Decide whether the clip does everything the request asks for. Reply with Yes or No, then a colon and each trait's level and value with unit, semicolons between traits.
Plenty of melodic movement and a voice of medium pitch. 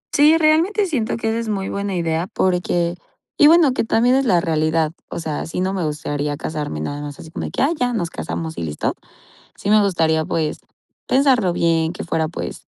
Yes: wide, 6.8 semitones; medium, 175 Hz